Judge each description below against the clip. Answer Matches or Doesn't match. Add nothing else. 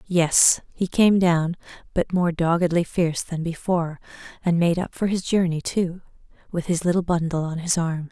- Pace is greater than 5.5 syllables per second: Doesn't match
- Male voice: Doesn't match